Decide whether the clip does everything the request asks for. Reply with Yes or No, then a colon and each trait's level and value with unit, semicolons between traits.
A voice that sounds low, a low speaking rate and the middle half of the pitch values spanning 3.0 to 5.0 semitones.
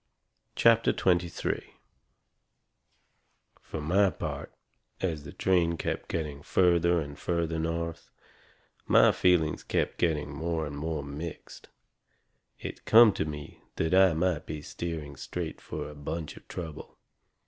No: very low, 80 Hz; slow, 125 wpm; narrow, 2.6 semitones